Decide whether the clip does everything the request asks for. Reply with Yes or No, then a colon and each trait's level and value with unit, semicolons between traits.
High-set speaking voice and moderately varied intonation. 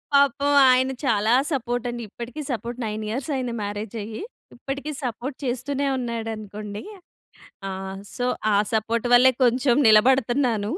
Yes: high, 240 Hz; average, 3.0 semitones